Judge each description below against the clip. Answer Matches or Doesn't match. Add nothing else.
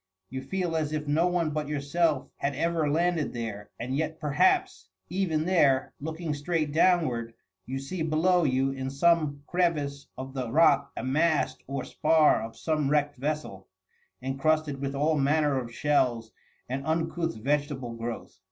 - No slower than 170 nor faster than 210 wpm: Doesn't match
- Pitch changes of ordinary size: Matches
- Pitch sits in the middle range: Matches